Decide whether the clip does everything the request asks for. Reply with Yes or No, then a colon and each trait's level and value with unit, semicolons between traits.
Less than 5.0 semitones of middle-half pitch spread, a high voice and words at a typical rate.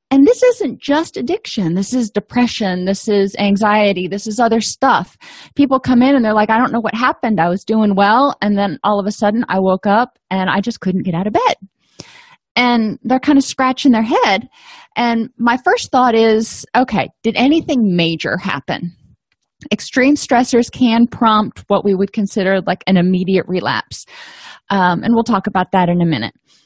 Yes: average, 4.6 semitones; high, 220 Hz; average, 190 wpm